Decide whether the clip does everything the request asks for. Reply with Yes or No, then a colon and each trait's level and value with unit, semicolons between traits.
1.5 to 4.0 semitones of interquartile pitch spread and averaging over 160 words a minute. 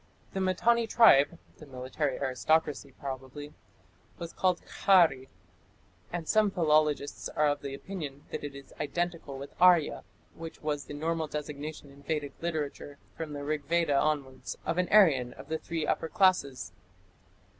No: average, 3.3 semitones; average, 145 wpm